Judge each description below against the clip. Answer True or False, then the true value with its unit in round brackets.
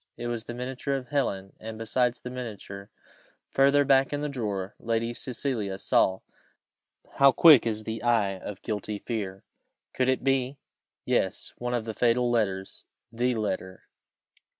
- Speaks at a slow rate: False (150 wpm)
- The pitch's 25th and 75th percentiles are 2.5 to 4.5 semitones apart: True (3.5 semitones)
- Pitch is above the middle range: False (120 Hz)